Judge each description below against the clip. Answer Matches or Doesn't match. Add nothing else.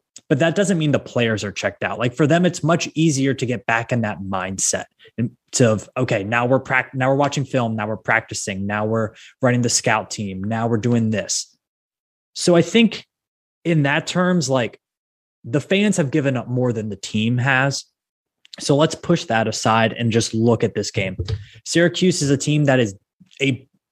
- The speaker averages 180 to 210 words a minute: Matches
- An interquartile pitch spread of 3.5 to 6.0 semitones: Matches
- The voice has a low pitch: Matches